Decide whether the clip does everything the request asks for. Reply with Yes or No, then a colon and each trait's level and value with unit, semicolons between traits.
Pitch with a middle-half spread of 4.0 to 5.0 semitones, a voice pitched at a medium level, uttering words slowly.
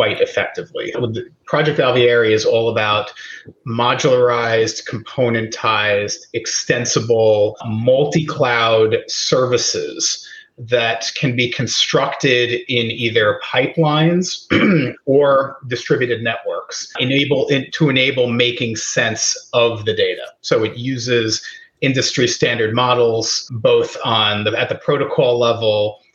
No: average, 4.4 semitones; low, 125 Hz; slow, 100 wpm